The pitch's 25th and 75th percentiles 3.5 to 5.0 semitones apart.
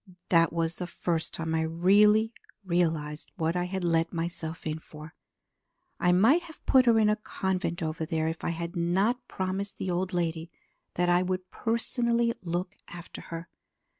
No: average, 3.1 semitones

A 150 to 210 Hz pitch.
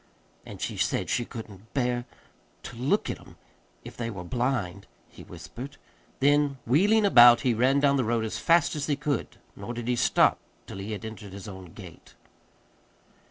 No: low, 120 Hz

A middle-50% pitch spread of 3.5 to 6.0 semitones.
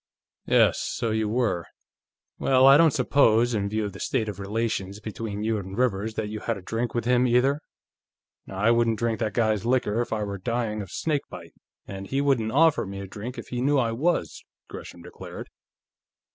No: average, 3.1 semitones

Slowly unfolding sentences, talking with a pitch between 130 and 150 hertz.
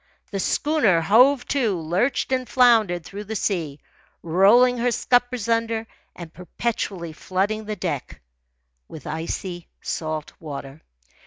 No: slow, 120 wpm; high, 200 Hz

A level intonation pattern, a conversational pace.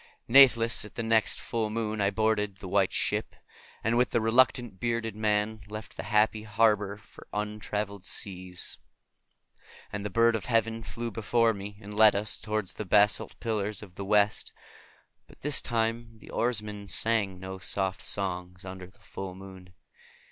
Yes: narrow, 2.3 semitones; average, 160 wpm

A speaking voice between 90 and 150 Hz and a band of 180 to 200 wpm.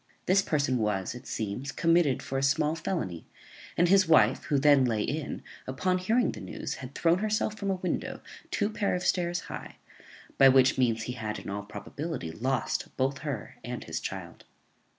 Yes: medium, 140 Hz; average, 185 wpm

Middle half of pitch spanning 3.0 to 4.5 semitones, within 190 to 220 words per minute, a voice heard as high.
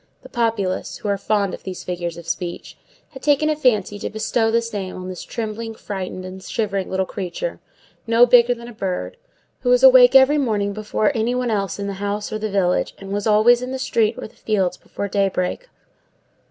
Yes: average, 3.7 semitones; fast, 205 wpm; high, 215 Hz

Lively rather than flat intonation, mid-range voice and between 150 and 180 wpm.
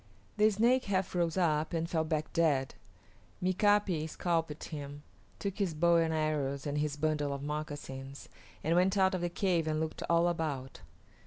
No: average, 3.1 semitones; medium, 160 Hz; average, 170 wpm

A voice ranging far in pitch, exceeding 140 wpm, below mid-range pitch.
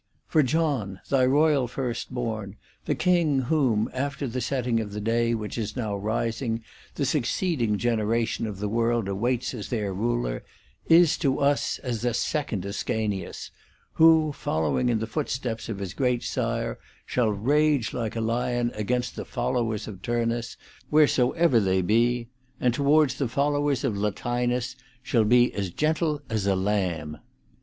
No: average, 3.8 semitones; average, 155 wpm; low, 120 Hz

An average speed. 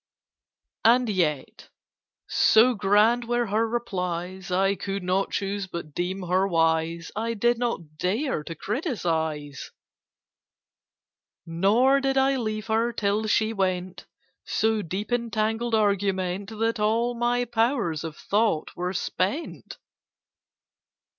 No: slow, 120 wpm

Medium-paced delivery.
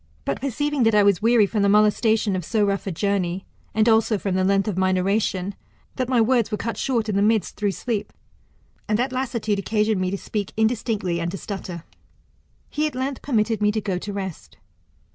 No: fast, 210 wpm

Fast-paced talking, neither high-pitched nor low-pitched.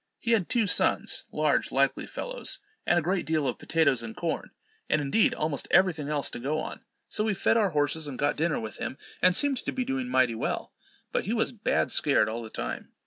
Yes: fast, 225 wpm; medium, 160 Hz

